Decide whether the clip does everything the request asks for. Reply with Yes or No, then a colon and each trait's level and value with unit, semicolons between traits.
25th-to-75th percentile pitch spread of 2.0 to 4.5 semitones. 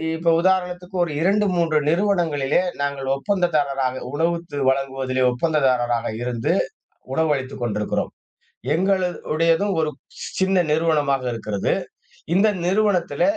No: average, 5.0 semitones